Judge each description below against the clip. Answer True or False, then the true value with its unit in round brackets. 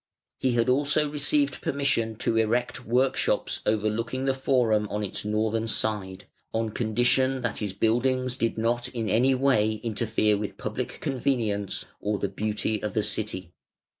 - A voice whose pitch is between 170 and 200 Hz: False (115 Hz)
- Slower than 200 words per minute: True (150 wpm)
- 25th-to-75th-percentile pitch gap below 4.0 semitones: True (3.2 semitones)